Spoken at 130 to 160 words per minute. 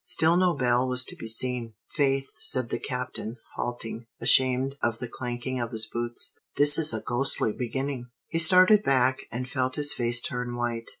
No: average, 180 wpm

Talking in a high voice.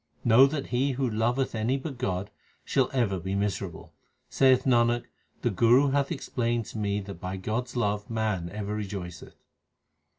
No: low, 115 Hz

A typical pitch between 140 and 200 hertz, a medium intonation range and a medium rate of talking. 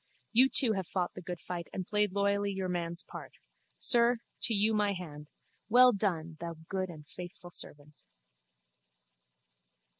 Yes: medium, 185 Hz; average, 3.3 semitones; average, 150 wpm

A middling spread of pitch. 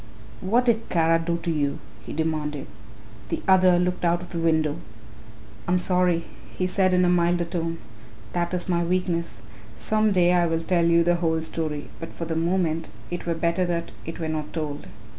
No: narrow, 1.7 semitones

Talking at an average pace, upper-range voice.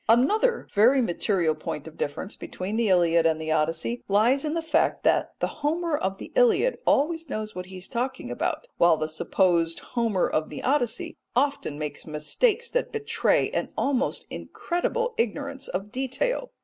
Yes: average, 170 wpm; high, 230 Hz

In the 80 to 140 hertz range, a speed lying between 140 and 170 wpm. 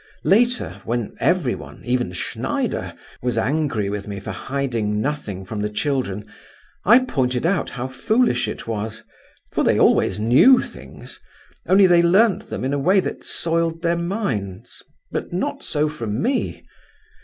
Yes: low, 135 Hz; average, 145 wpm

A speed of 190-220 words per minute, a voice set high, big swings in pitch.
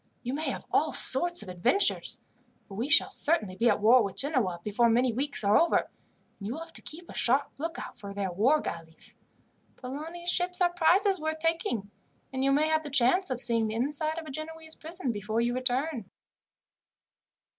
Yes: average, 195 wpm; very high, 270 Hz; wide, 6.2 semitones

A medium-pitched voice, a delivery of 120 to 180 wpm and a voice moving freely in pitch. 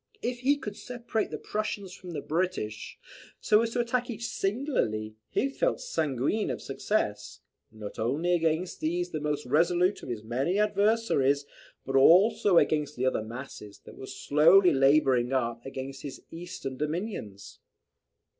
Yes: medium, 160 Hz; average, 150 wpm; wide, 7.8 semitones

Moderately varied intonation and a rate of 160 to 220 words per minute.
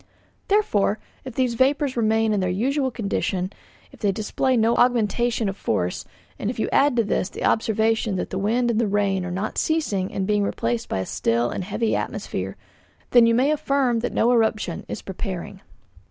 Yes: average, 3.9 semitones; average, 185 wpm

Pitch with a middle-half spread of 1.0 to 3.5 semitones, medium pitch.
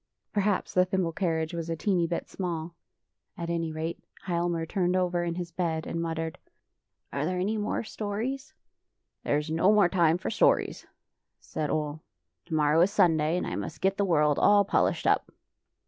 Yes: average, 2.8 semitones; medium, 170 Hz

